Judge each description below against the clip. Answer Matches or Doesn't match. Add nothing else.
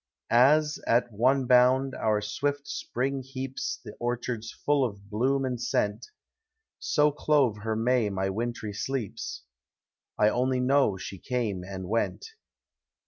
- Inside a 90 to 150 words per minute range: Matches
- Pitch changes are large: Doesn't match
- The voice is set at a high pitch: Doesn't match